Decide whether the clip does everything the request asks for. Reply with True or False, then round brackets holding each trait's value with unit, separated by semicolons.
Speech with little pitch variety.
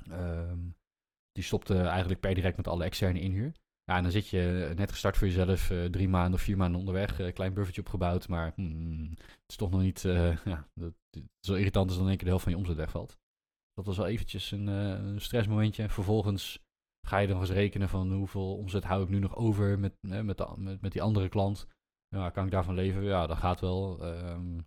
True (1.9 semitones)